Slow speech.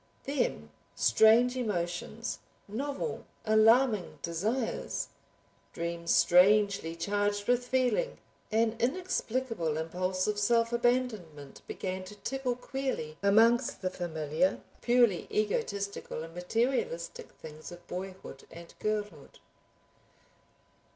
Yes: slow, 95 wpm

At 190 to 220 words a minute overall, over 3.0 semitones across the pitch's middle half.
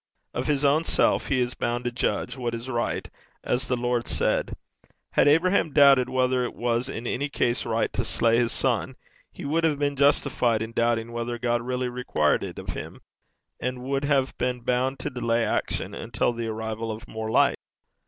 No: average, 195 wpm; narrow, 2.5 semitones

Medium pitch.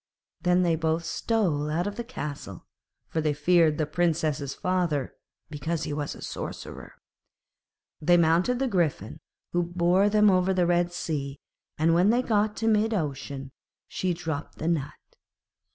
Yes: medium, 170 Hz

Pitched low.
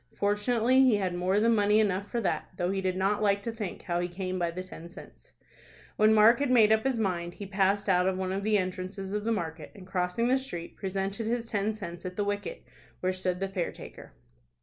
No: high, 195 Hz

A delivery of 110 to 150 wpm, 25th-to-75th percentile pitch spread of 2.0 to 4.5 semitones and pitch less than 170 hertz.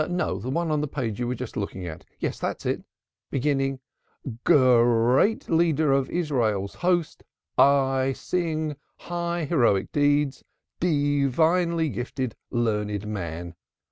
No: slow, 135 wpm; average, 5.1 semitones; low, 135 Hz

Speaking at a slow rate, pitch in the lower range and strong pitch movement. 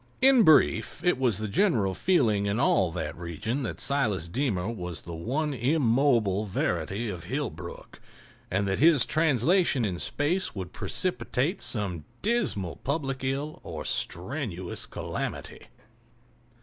Yes: slow, 130 wpm; low, 120 Hz; wide, 7.2 semitones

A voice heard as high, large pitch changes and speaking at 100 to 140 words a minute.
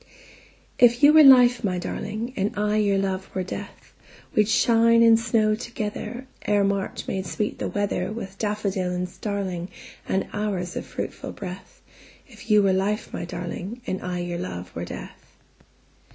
No: high, 205 Hz; average, 3.2 semitones; slow, 135 wpm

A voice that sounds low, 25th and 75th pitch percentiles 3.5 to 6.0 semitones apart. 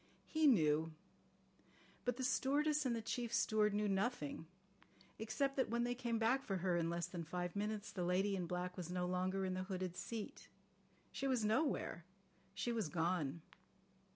No: high, 200 Hz; average, 4.9 semitones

